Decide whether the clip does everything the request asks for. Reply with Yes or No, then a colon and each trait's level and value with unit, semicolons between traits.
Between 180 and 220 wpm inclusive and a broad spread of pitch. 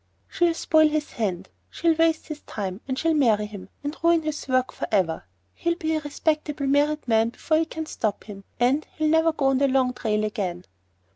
Yes: average, 200 wpm; wide, 6.3 semitones